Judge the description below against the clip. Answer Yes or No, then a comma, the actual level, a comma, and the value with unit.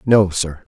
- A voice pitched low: Yes, very low, 95 Hz